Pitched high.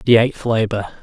No: low, 115 Hz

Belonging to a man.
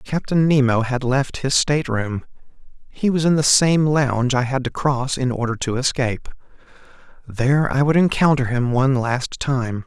Yes: male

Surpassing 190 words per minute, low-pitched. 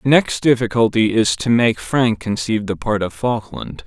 No: average, 185 wpm; low, 115 Hz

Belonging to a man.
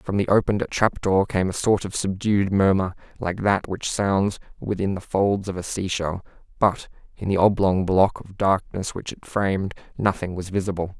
Yes: male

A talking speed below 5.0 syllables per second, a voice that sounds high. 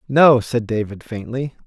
No: 4.2 syllables/s; low, 120 Hz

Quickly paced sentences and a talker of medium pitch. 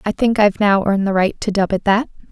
No: fast, 285 wpm; high, 205 Hz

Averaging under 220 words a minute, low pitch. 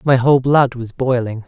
Yes: fast, 205 wpm; low, 125 Hz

